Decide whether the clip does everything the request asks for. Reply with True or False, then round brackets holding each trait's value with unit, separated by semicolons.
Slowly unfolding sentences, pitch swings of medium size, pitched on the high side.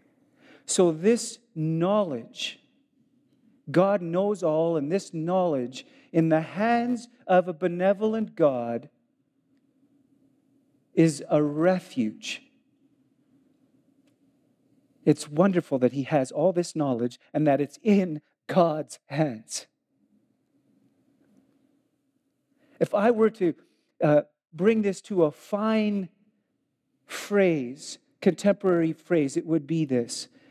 False (100 wpm; 8.9 semitones; 205 Hz)